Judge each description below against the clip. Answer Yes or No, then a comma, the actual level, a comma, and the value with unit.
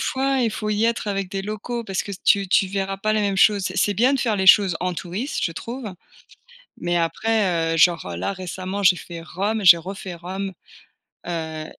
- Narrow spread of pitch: No, average, 3.3 semitones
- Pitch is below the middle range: No, high, 195 Hz